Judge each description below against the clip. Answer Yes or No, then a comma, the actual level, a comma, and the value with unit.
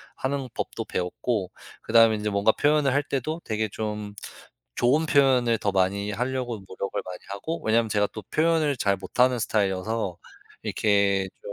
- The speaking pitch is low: Yes, low, 110 Hz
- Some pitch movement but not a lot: Yes, average, 4.5 semitones